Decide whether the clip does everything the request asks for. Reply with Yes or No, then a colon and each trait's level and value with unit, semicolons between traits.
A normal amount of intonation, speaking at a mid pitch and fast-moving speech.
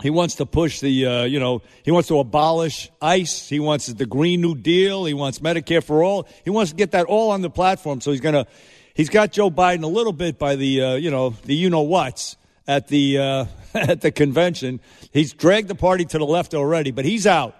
Yes: average, 4.1 semitones; medium, 155 Hz; fast, 235 wpm